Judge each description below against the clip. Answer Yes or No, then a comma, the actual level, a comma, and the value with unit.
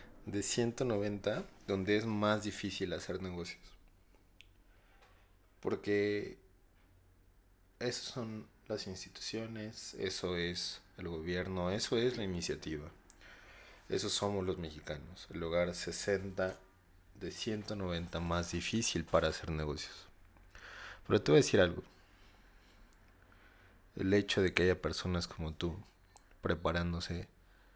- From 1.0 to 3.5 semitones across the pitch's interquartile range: Yes, narrow, 2.6 semitones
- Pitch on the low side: Yes, very low, 95 Hz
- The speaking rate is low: Yes, slow, 110 wpm